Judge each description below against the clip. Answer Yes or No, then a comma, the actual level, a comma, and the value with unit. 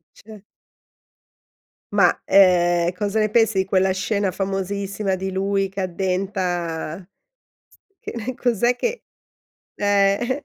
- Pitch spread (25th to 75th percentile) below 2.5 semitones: Yes, narrow, 2.1 semitones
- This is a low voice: No, high, 195 Hz